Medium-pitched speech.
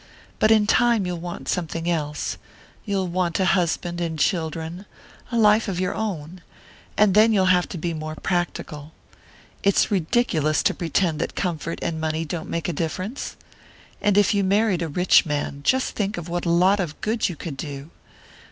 Yes: medium, 175 Hz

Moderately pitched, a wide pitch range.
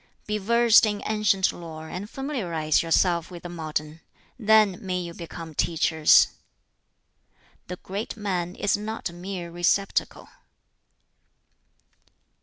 No: medium, 180 Hz; average, 3.6 semitones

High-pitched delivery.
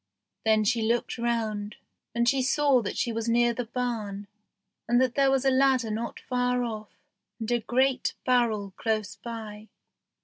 Yes: high, 235 Hz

